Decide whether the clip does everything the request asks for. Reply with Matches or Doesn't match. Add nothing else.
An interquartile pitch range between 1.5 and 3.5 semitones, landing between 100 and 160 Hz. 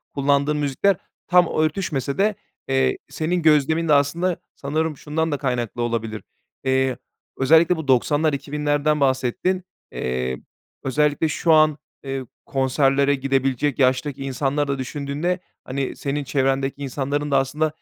Matches